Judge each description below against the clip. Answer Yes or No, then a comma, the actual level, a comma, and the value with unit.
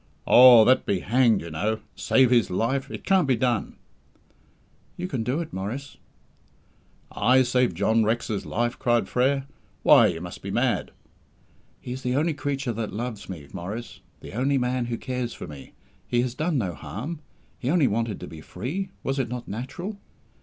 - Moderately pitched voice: No, low, 125 Hz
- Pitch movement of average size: Yes, average, 3.4 semitones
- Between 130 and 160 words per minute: No, average, 180 wpm